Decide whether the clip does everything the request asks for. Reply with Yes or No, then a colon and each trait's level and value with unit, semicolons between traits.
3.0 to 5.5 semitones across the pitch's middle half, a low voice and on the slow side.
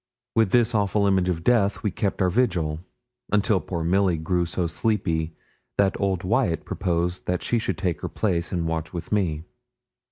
No: average, 3.3 semitones; very low, 90 Hz; average, 180 wpm